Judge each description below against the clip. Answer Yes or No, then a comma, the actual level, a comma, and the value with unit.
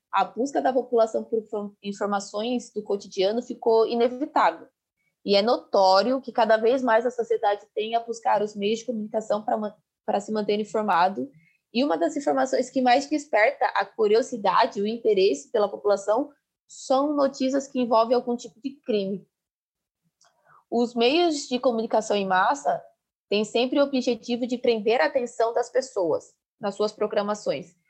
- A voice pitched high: Yes, high, 230 Hz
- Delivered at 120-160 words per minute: Yes, average, 155 wpm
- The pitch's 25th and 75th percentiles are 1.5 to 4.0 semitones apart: Yes, average, 3.7 semitones